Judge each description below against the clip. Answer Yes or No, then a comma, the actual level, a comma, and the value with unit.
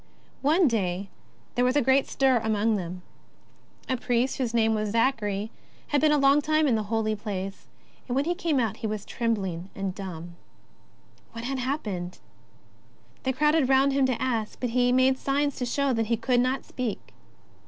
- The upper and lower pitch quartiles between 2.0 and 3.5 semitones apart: No, average, 4.2 semitones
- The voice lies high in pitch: Yes, high, 240 Hz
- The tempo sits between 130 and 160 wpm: No, average, 185 wpm